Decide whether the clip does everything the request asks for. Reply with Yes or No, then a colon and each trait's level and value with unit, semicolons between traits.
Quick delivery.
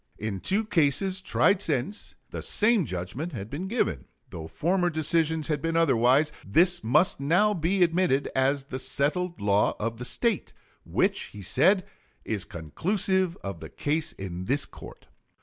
No: average, 155 wpm